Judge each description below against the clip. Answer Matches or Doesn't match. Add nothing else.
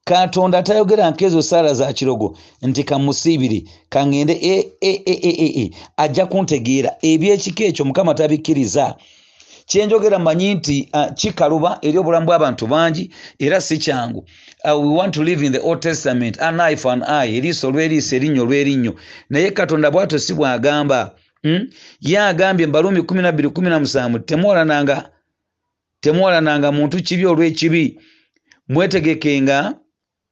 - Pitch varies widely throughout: Doesn't match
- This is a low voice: Doesn't match